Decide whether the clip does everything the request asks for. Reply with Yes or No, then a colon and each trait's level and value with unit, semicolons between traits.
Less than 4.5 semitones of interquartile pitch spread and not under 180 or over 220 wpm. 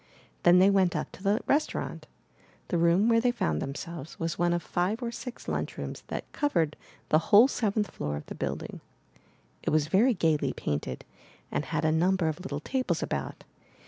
No: wide, 5.4 semitones; average, 185 wpm